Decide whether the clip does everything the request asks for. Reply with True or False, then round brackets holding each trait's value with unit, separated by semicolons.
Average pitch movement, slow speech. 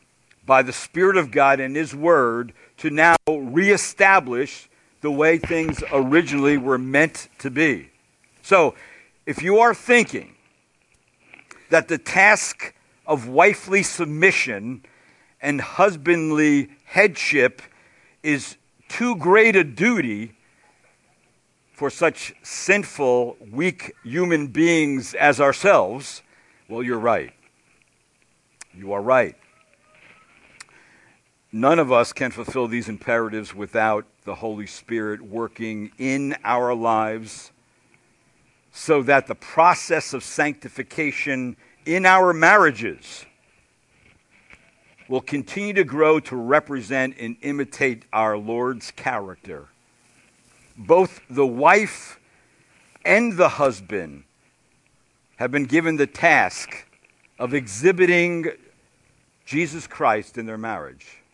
False (5.7 semitones; 105 wpm)